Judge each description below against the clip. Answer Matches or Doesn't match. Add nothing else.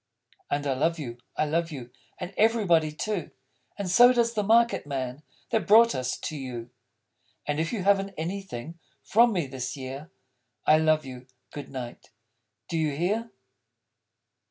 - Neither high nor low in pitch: Matches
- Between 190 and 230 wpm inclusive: Doesn't match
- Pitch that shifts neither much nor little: Doesn't match